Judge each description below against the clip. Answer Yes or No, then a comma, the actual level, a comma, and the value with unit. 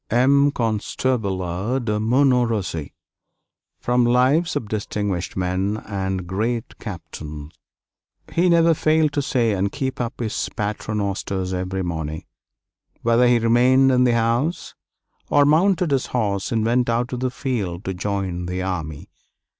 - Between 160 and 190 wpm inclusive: No, average, 140 wpm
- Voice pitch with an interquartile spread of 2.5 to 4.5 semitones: No, average, 5.1 semitones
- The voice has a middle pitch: No, low, 115 Hz